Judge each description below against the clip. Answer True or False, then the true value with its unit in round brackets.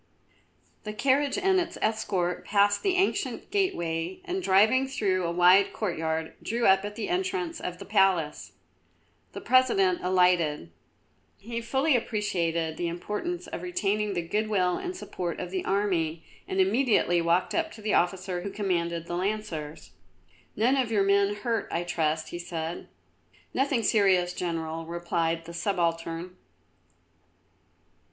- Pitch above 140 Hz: True (190 Hz)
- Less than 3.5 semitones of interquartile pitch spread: False (4.6 semitones)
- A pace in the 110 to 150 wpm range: True (145 wpm)